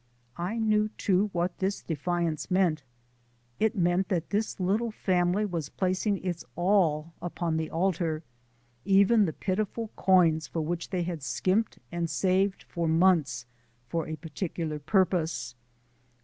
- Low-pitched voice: No, medium, 180 Hz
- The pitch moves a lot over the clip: No, average, 3.0 semitones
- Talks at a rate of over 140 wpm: No, slow, 135 wpm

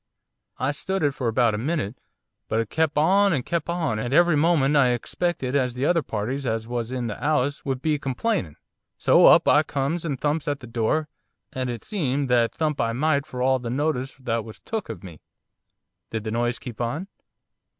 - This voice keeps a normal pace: No, fast, 210 wpm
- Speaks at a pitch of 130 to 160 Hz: Yes, low, 135 Hz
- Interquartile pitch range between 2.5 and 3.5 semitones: No, average, 4.5 semitones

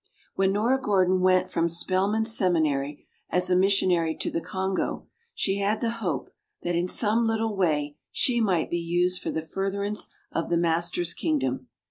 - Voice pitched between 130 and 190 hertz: Yes, medium, 185 Hz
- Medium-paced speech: Yes, average, 165 wpm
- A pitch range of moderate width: Yes, average, 3.2 semitones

